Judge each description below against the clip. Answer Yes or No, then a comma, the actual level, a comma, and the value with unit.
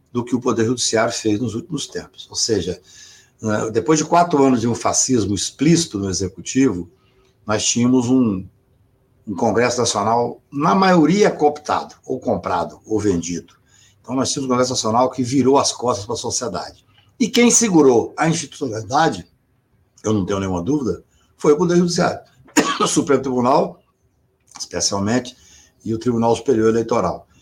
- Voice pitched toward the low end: Yes, low, 125 Hz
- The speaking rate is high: No, average, 155 wpm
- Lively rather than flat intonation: No, average, 4.6 semitones